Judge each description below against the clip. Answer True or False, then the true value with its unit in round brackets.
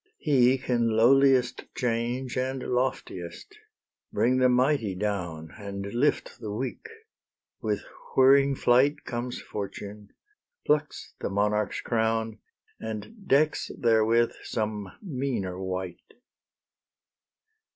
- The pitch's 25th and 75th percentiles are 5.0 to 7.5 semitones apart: False (4.0 semitones)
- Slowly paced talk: True (100 wpm)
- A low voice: True (120 Hz)